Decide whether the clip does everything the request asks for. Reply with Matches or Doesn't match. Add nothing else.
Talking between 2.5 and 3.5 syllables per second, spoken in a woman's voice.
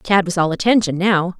Doesn't match